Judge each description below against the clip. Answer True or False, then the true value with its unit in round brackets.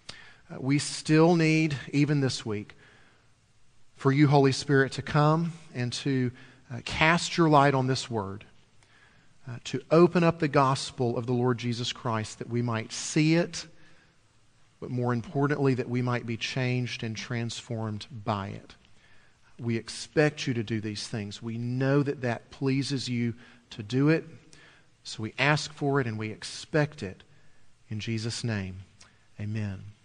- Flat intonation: False (4.2 semitones)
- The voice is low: True (125 Hz)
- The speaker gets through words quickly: False (160 wpm)